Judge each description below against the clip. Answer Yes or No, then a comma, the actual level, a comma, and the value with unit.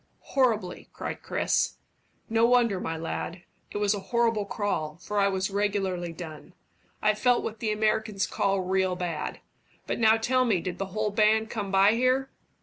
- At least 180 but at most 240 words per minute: No, average, 170 wpm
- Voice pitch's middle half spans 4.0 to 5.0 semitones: No, average, 3.0 semitones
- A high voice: Yes, high, 205 Hz